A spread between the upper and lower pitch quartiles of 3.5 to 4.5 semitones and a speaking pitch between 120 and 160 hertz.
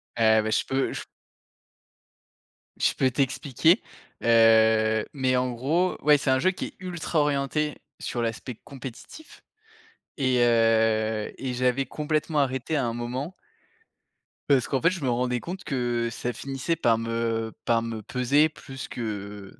Yes: average, 3.8 semitones; low, 125 Hz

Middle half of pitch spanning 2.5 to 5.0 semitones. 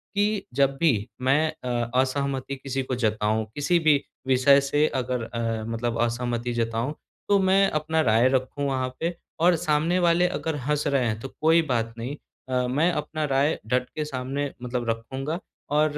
Yes: average, 4.0 semitones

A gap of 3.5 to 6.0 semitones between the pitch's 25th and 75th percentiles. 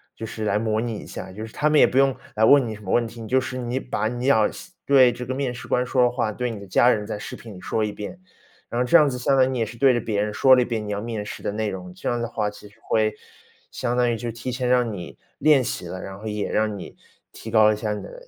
No: average, 2.9 semitones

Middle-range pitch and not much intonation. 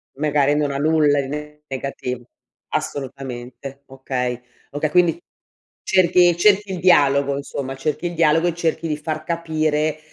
No: medium, 150 Hz; average, 3.1 semitones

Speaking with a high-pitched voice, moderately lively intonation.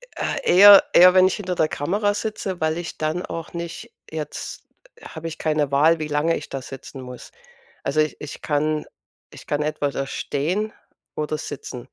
No: medium, 155 Hz; average, 3.2 semitones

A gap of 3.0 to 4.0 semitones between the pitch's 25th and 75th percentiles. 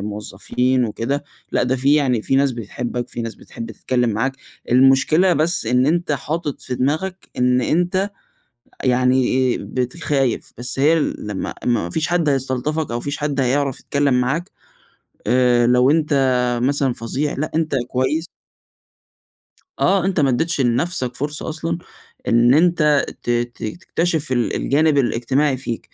Yes: average, 3.6 semitones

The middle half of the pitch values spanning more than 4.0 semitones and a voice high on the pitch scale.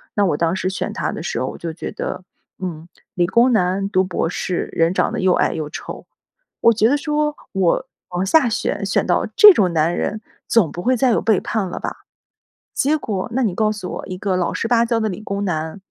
Yes: average, 4.4 semitones; high, 195 Hz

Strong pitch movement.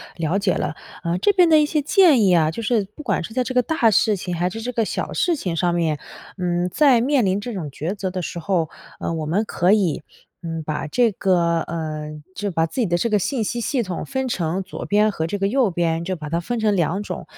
Yes: wide, 5.7 semitones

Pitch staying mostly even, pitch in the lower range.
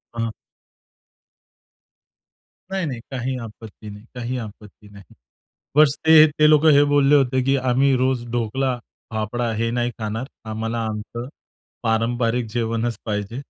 No: average, 3.0 semitones; low, 120 Hz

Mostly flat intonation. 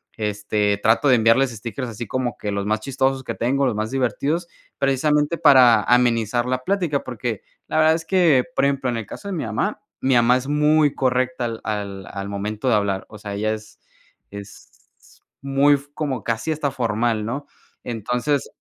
No: average, 4.3 semitones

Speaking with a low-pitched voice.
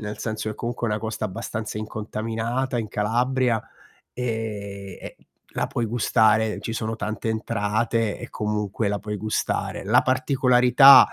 Yes: low, 110 Hz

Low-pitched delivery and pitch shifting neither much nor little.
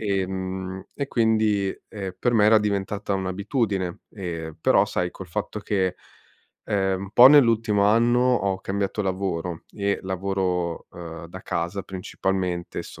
No: very low, 95 Hz; narrow, 2.1 semitones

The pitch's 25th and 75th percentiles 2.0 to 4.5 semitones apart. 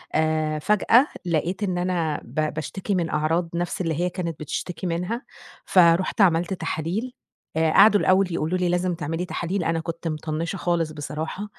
Yes: narrow, 2.5 semitones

